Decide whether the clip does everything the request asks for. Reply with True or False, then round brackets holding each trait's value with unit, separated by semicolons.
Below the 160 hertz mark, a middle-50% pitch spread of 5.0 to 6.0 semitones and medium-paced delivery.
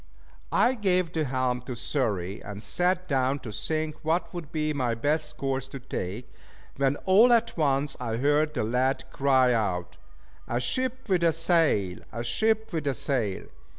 True (140 Hz; 5.3 semitones; 170 wpm)